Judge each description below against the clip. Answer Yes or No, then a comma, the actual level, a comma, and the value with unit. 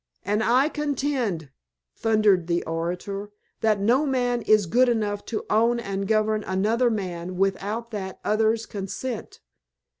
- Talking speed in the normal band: No, slow, 130 wpm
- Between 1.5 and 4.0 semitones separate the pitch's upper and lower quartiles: Yes, average, 3.4 semitones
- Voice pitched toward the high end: Yes, high, 215 Hz